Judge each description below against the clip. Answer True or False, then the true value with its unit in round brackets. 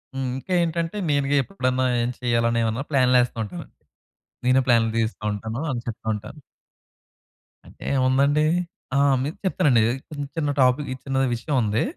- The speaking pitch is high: False (130 Hz)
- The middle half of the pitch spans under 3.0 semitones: False (3.6 semitones)